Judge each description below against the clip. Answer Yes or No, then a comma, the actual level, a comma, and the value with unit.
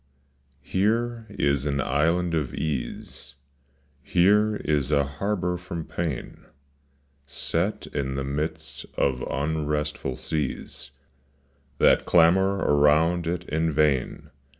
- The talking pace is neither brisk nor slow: No, slow, 105 wpm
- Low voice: Yes, very low, 80 Hz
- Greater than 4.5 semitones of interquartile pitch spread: No, average, 3.7 semitones